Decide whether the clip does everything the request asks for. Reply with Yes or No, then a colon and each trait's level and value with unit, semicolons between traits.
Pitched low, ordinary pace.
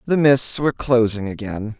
Yes: low, 120 Hz; average, 165 wpm